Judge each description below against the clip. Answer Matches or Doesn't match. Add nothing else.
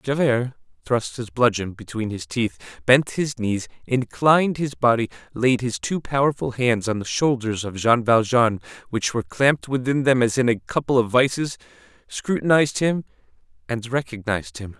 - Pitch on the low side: Matches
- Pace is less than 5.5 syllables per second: Matches